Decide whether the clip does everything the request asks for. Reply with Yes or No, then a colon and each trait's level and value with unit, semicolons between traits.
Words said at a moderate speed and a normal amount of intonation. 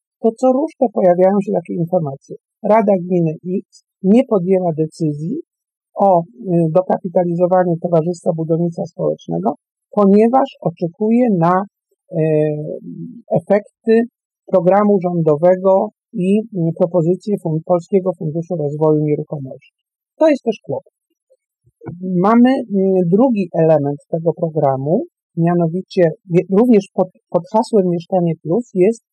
No: slow, 95 wpm; average, 3.9 semitones